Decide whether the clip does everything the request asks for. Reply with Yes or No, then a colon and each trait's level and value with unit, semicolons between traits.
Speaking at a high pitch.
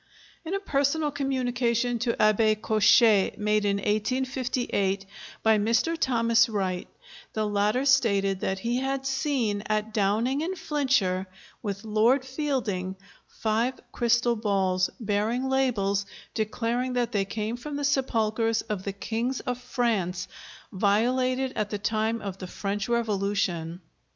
Yes: high, 225 Hz